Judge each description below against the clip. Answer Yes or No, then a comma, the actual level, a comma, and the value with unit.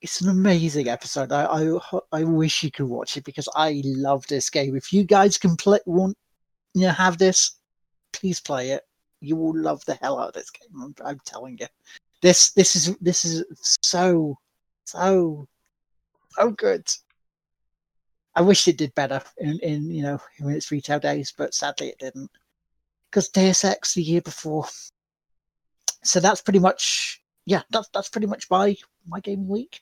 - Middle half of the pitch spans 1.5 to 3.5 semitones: No, average, 4.5 semitones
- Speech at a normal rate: Yes, average, 175 wpm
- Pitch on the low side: No, medium, 170 Hz